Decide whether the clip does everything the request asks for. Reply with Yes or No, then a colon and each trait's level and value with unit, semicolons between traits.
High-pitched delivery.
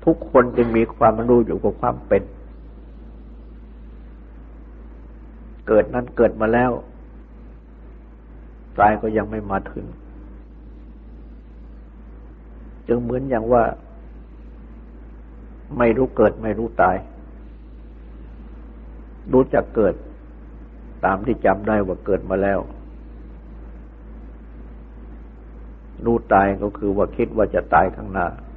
No: very low, 95 Hz